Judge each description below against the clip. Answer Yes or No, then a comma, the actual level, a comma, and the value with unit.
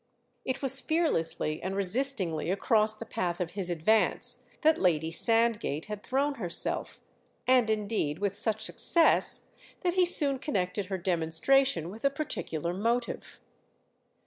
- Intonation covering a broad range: Yes, wide, 7.1 semitones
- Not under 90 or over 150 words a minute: Yes, slow, 135 wpm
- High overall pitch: Yes, high, 210 Hz